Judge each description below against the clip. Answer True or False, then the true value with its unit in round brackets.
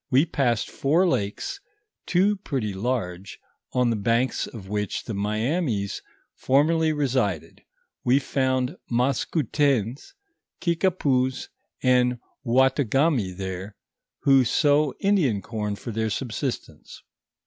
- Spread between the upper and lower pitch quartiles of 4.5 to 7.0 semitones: True (5.1 semitones)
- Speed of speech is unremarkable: False (105 wpm)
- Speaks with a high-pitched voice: False (125 Hz)